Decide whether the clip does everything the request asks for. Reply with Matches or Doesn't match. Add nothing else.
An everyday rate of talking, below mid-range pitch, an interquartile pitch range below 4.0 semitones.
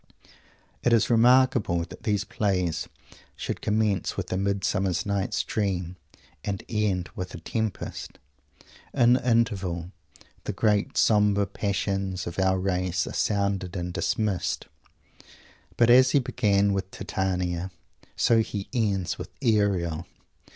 Doesn't match